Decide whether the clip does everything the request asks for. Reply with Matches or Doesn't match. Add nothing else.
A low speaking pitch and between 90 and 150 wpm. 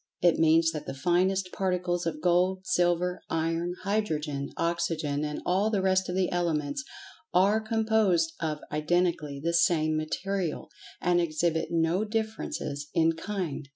Doesn't match